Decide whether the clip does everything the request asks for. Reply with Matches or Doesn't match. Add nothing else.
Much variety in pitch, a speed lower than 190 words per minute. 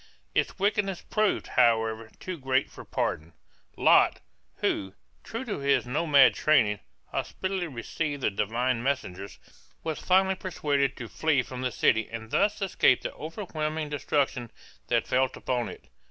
Matches